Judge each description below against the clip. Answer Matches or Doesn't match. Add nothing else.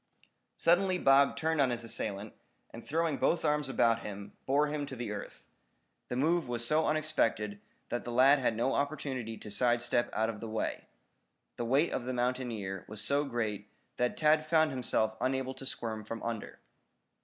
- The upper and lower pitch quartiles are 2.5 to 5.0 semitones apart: Matches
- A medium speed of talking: Matches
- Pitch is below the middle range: Matches